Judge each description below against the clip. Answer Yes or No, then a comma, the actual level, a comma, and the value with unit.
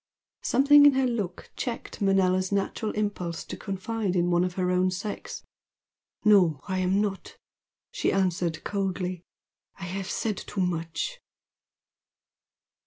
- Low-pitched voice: No, high, 190 Hz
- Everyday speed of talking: No, slow, 130 wpm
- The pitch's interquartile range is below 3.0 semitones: Yes, narrow, 2.5 semitones